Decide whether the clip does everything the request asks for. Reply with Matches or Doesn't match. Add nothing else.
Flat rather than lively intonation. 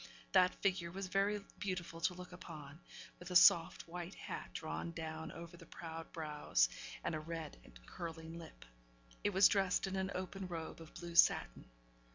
Matches